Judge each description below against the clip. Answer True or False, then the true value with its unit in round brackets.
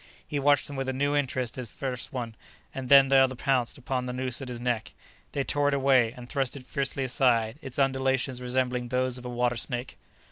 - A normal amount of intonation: False (1.6 semitones)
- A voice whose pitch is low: True (130 Hz)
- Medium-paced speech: False (220 wpm)